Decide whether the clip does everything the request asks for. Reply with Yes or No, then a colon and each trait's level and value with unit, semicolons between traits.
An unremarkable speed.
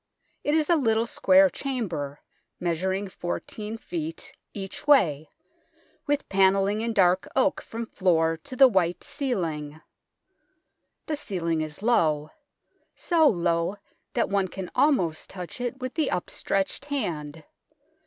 No: slow, 125 wpm